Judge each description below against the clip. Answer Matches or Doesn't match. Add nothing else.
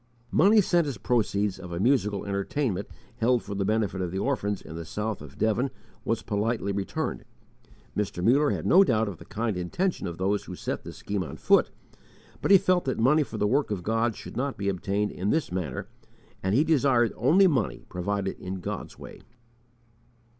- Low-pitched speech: Matches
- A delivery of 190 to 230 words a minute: Matches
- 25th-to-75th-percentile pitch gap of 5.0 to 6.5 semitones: Matches